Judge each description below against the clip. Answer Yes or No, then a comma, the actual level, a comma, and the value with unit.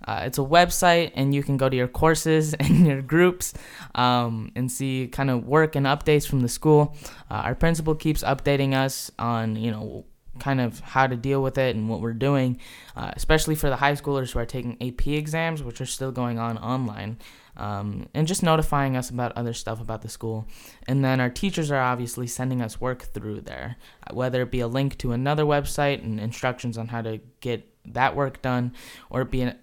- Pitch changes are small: No, average, 3.1 semitones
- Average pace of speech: No, fast, 215 wpm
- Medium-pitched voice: No, low, 130 Hz